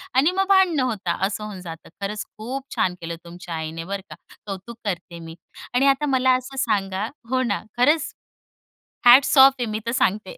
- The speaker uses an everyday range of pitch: No, wide, 6.1 semitones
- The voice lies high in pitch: Yes, high, 215 Hz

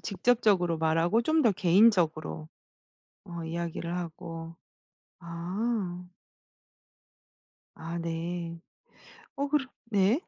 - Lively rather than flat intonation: No, average, 4.2 semitones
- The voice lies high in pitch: No, medium, 175 Hz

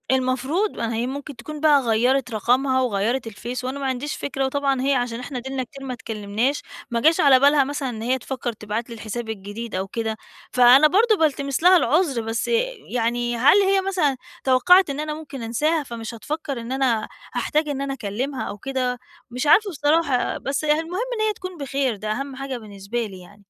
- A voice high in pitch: Yes, very high, 260 Hz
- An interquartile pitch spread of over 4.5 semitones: No, average, 3.7 semitones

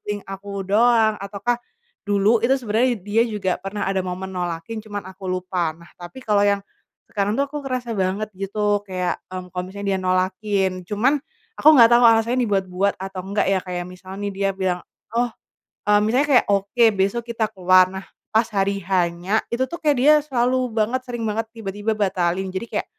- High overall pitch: Yes, high, 200 Hz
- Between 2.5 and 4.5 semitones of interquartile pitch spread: Yes, average, 3.3 semitones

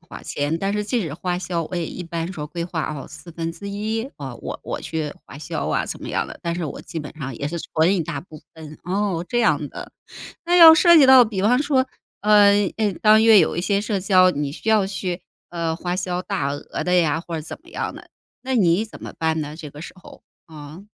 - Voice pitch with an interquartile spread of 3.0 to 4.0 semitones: No, average, 4.6 semitones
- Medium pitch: Yes, medium, 175 Hz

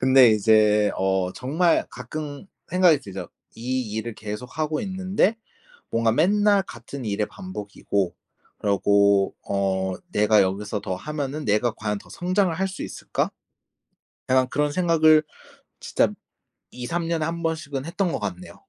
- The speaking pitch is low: Yes, low, 125 Hz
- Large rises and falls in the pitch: Yes, wide, 7.8 semitones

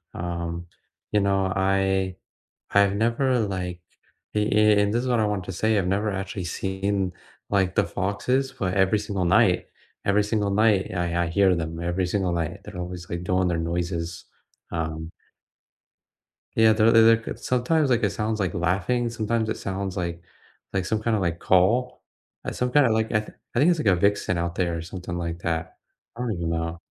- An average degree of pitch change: Yes, average, 3.7 semitones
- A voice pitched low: Yes, very low, 95 Hz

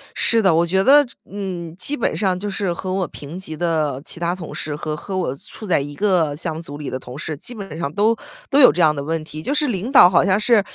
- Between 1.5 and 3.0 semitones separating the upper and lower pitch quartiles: No, average, 4.6 semitones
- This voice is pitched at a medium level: Yes, medium, 175 Hz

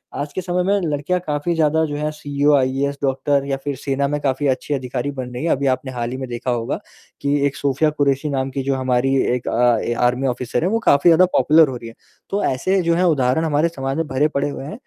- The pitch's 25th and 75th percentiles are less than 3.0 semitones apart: Yes, narrow, 2.6 semitones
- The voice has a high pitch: No, medium, 140 Hz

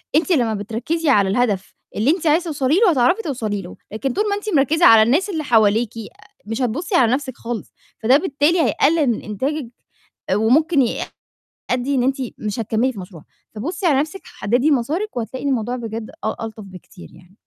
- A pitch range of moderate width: No, wide, 5.9 semitones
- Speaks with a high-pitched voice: Yes, very high, 250 Hz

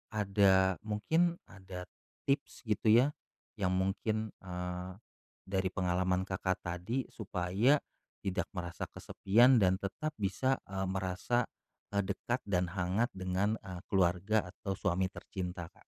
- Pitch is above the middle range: No, very low, 95 Hz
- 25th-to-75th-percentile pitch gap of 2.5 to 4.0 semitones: Yes, average, 2.8 semitones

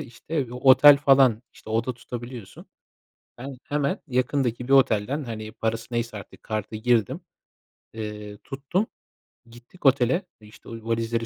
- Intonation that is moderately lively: Yes, average, 3.2 semitones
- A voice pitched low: Yes, low, 120 Hz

